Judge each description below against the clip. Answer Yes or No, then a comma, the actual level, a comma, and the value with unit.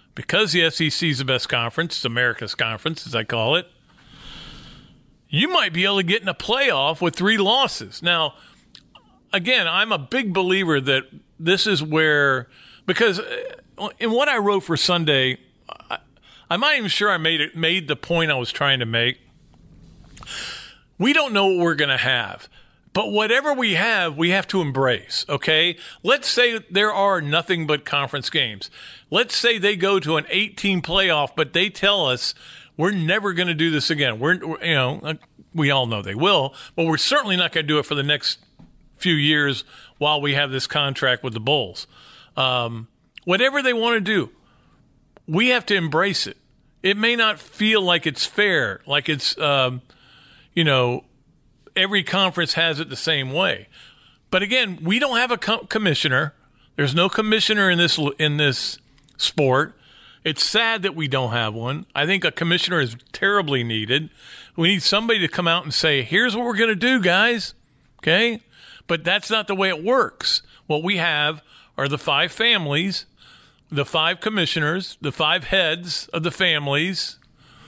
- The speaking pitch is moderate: Yes, medium, 165 Hz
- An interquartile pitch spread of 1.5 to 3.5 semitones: No, wide, 5.5 semitones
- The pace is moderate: Yes, average, 180 wpm